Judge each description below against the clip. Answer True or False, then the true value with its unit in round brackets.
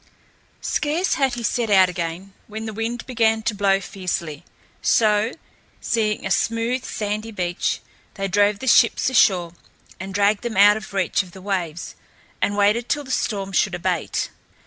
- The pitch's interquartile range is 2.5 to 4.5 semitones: True (3.1 semitones)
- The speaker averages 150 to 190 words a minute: True (165 wpm)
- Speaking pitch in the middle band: False (205 Hz)